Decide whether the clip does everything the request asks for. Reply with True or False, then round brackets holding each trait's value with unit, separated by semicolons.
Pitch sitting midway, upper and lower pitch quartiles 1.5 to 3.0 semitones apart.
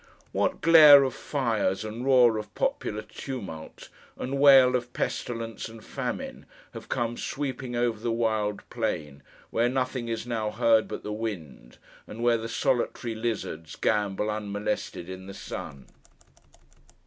False (115 Hz; 2.7 semitones)